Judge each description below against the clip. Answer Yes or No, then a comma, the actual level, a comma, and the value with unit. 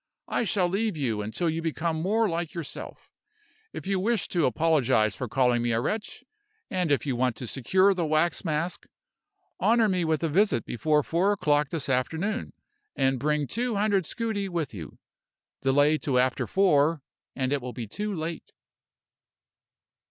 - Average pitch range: No, wide, 6.1 semitones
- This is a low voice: No, medium, 160 Hz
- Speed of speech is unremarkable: Yes, average, 165 wpm